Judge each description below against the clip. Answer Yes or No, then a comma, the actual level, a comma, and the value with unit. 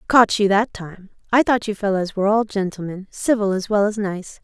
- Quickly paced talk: Yes, fast, 215 wpm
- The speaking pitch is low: No, high, 205 Hz